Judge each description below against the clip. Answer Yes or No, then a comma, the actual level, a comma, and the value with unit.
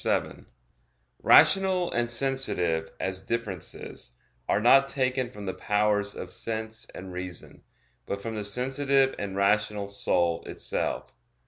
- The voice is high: No, low, 105 Hz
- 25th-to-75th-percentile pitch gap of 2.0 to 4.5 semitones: No, average, 4.9 semitones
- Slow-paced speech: Yes, slow, 125 wpm